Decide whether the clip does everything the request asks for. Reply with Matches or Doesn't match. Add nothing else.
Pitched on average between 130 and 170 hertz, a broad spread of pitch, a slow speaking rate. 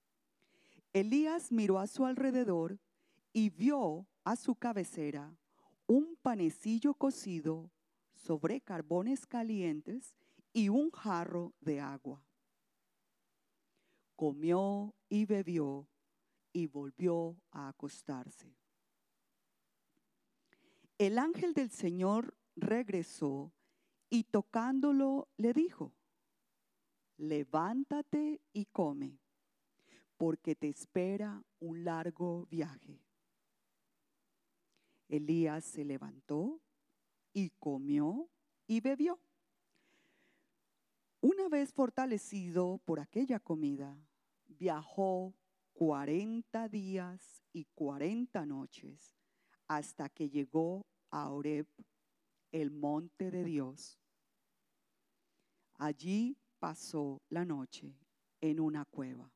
Doesn't match